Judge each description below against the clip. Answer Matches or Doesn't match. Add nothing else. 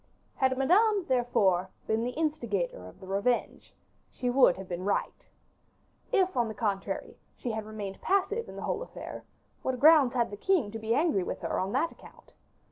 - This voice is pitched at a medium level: Doesn't match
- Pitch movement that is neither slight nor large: Doesn't match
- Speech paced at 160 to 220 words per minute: Matches